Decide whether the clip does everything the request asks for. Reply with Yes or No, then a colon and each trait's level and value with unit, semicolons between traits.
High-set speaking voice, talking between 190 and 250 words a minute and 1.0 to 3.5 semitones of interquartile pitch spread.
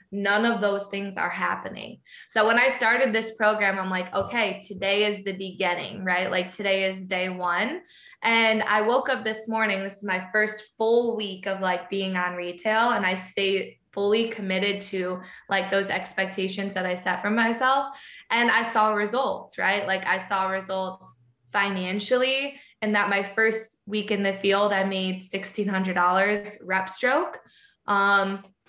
No: high, 200 Hz; average, 165 wpm; narrow, 2.5 semitones